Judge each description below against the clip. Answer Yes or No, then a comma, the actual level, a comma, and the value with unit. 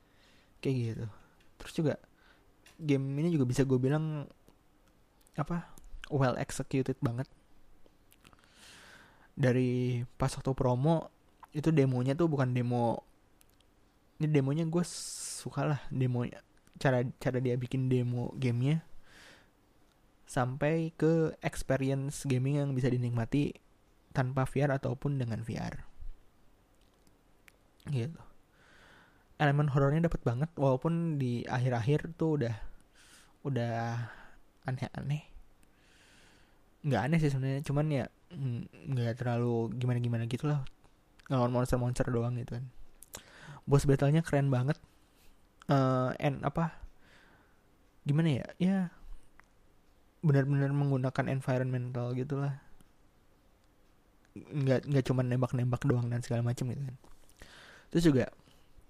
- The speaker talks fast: No, average, 105 wpm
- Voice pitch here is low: Yes, low, 130 Hz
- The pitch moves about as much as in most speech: Yes, average, 3.0 semitones